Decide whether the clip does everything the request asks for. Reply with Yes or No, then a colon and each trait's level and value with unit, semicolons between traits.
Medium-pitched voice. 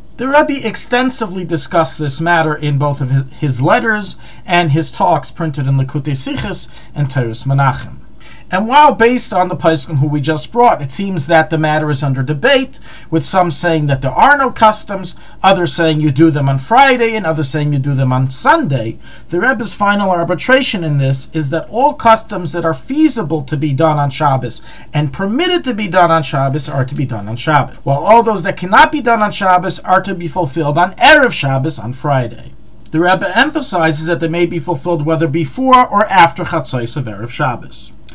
Yes: medium, 165 Hz